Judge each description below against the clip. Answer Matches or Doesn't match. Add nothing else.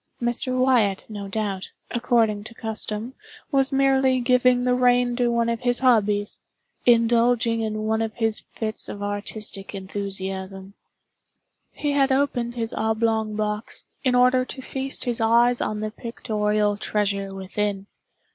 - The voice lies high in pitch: Matches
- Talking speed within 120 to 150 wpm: Matches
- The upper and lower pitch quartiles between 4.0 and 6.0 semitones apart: Doesn't match